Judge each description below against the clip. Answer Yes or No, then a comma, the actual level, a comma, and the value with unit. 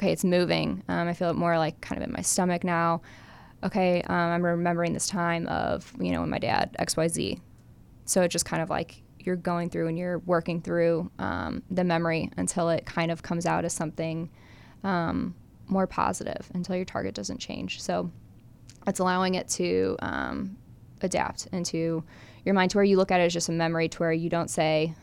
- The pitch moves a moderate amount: No, narrow, 1.7 semitones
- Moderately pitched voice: Yes, medium, 170 Hz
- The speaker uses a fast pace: Yes, fast, 210 wpm